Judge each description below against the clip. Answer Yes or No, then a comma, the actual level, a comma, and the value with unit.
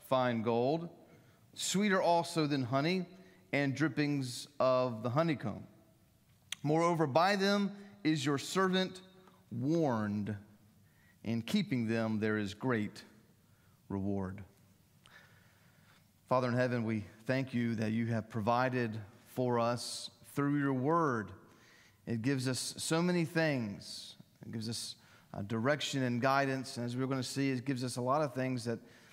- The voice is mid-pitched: No, low, 130 Hz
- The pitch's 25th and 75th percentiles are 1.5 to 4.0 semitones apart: No, average, 4.9 semitones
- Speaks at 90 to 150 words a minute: Yes, average, 140 wpm